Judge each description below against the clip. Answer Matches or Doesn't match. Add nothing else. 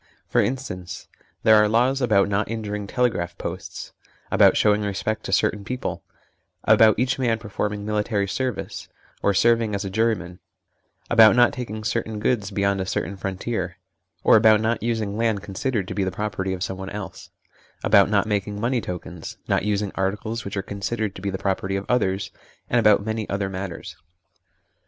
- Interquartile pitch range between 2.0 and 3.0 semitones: Matches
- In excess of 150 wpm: Matches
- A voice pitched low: Matches